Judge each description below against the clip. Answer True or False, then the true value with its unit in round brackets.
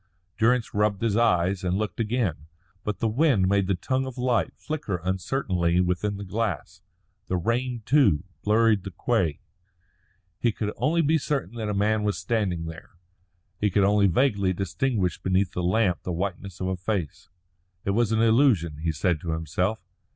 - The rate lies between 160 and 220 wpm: True (175 wpm)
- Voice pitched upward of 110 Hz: False (100 Hz)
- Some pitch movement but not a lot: True (4.1 semitones)